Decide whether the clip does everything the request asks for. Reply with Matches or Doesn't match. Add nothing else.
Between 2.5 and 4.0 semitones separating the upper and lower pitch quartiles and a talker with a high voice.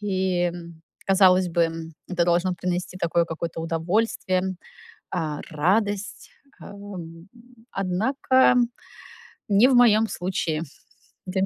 Doesn't match